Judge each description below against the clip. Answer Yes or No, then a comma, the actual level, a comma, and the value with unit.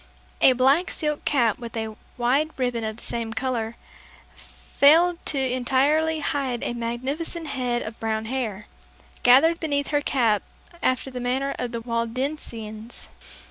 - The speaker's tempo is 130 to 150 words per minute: Yes, average, 140 wpm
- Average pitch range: Yes, average, 3.5 semitones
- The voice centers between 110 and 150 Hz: No, very high, 255 Hz